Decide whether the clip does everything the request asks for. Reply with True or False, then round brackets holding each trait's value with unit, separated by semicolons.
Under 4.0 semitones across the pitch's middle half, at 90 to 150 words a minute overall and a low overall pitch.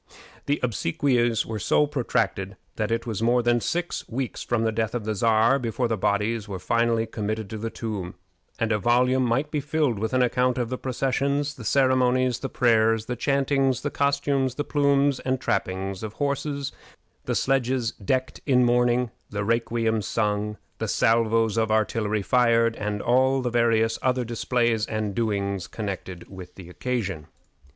False (2.9 semitones; 170 wpm; 115 Hz)